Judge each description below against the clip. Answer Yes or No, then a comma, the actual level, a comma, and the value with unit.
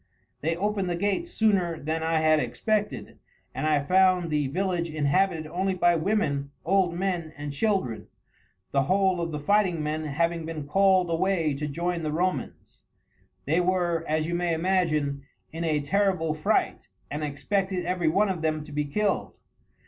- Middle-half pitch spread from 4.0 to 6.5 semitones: No, average, 3.5 semitones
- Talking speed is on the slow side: No, average, 165 wpm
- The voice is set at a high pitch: No, medium, 170 Hz